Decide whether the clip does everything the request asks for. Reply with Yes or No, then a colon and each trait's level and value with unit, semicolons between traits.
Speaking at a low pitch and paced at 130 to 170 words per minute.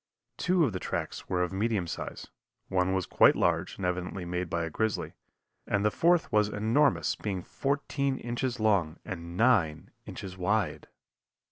Yes: low, 100 Hz; average, 160 wpm